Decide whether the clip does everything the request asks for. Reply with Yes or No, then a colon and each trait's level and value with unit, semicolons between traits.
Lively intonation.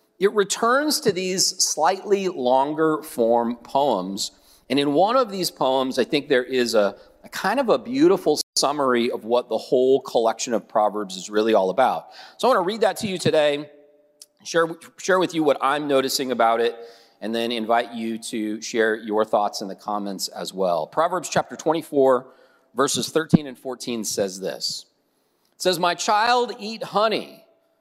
Yes: wide, 7.6 semitones